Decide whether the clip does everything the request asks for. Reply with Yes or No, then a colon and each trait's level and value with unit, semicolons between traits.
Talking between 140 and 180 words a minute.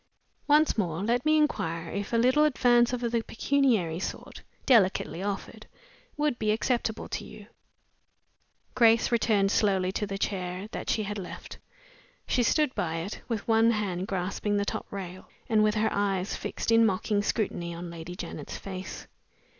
Yes: average, 160 wpm